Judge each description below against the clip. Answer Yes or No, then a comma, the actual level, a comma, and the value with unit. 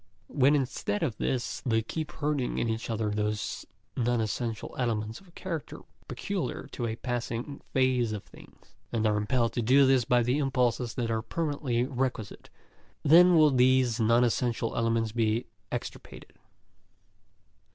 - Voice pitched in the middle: No, low, 120 Hz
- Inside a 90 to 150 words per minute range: Yes, average, 145 wpm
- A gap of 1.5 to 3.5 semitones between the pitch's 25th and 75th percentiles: Yes, average, 2.8 semitones